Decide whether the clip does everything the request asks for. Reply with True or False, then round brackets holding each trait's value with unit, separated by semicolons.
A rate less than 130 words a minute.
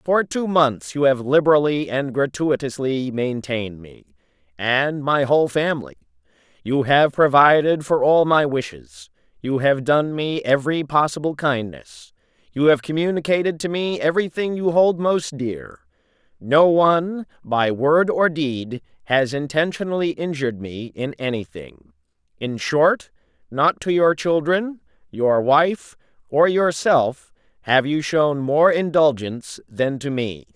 False (135 wpm)